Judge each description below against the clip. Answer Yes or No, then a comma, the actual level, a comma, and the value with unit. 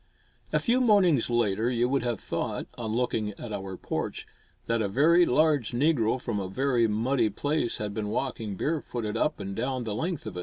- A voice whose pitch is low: Yes, low, 120 Hz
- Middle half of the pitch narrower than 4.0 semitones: No, average, 4.5 semitones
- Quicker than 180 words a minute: Yes, average, 200 wpm